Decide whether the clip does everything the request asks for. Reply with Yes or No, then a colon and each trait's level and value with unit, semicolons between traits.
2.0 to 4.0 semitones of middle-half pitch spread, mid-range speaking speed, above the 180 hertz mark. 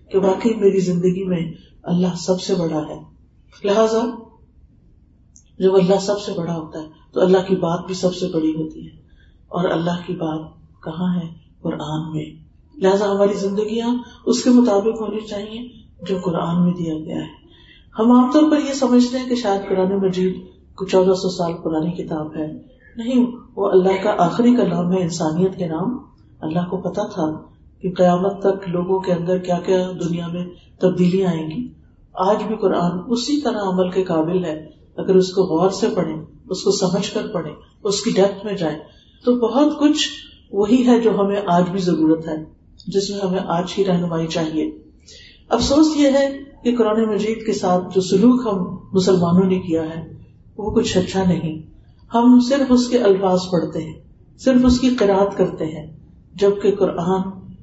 Yes: average, 3.6 semitones; average, 180 wpm; high, 190 Hz